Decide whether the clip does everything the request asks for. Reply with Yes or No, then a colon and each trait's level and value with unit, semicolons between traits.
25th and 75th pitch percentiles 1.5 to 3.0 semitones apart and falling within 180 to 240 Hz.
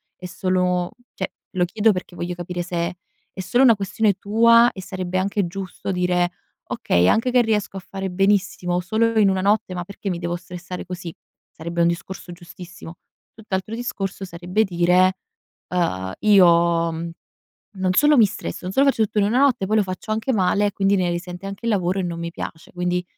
Yes: average, 2.7 semitones; medium, 185 Hz